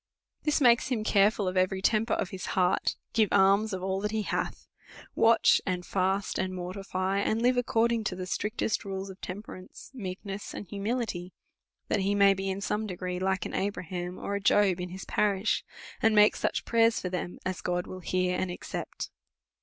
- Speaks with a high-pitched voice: Yes, high, 195 Hz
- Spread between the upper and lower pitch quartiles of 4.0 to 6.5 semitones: No, narrow, 2.5 semitones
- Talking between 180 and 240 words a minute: Yes, average, 190 wpm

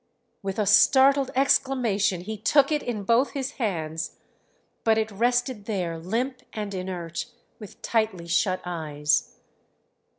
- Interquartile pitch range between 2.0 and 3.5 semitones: No, wide, 5.4 semitones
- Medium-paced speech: No, slow, 130 wpm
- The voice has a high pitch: Yes, high, 215 Hz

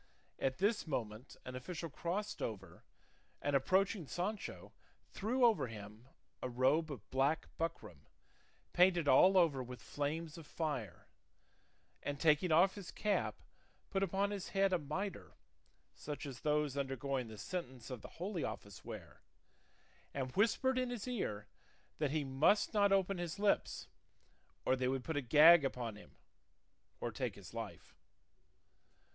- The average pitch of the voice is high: No, medium, 155 Hz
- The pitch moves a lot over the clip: Yes, wide, 6.7 semitones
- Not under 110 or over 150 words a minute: Yes, average, 145 wpm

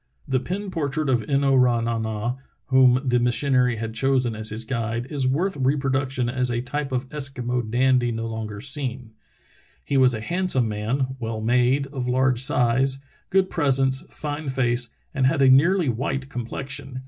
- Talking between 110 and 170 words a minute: No, average, 185 wpm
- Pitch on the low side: Yes, low, 130 Hz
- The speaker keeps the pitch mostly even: Yes, narrow, 2.3 semitones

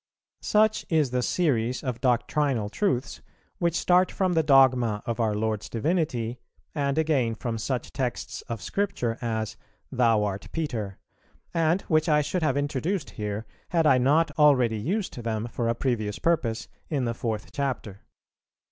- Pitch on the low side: Yes, low, 130 Hz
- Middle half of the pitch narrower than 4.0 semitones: No, wide, 5.5 semitones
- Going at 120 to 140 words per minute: No, average, 155 wpm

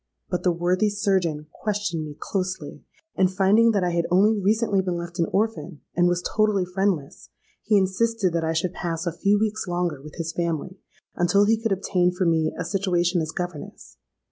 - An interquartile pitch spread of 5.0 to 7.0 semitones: No, average, 2.9 semitones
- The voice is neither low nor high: Yes, medium, 180 Hz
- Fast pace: No, average, 190 wpm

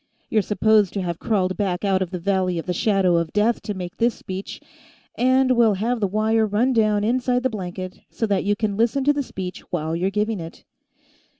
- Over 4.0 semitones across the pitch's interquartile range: No, average, 3.3 semitones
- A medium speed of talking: No, fast, 215 wpm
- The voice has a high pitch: Yes, high, 205 Hz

